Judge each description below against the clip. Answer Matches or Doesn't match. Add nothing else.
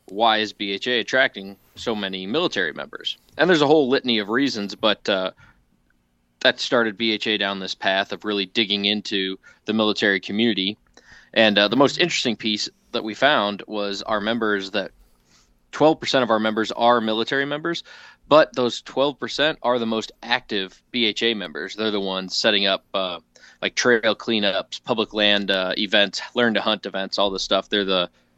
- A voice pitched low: Matches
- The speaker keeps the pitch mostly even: Doesn't match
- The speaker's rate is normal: Matches